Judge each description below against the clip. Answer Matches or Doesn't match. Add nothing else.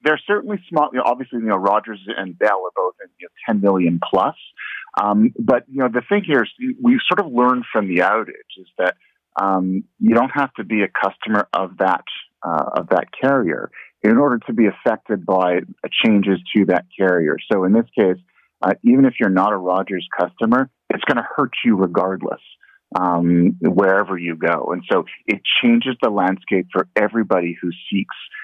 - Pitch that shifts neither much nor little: Doesn't match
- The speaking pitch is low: Matches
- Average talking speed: Matches